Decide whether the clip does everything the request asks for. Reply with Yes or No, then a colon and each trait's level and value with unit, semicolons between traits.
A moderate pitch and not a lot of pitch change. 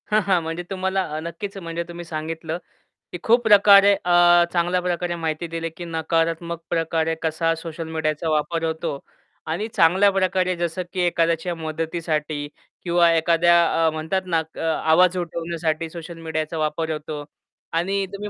Yes: medium, 170 Hz; narrow, 1.7 semitones